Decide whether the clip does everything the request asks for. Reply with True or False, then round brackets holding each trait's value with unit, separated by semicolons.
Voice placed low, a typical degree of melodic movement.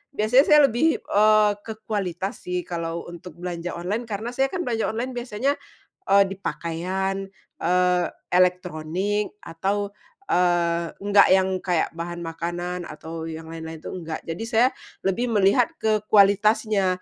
False (190 Hz; 3.7 semitones)